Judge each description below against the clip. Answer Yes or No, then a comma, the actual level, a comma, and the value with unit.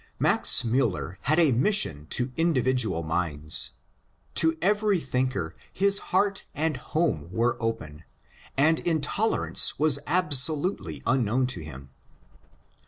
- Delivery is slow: Yes, slow, 110 wpm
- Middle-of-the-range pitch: No, low, 130 Hz